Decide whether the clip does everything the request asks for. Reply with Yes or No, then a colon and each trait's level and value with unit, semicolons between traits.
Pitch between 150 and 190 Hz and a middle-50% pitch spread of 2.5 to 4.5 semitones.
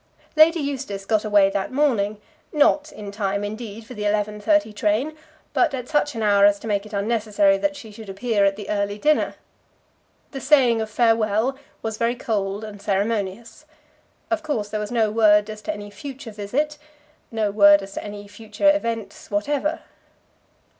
No: high, 215 Hz; average, 3.5 semitones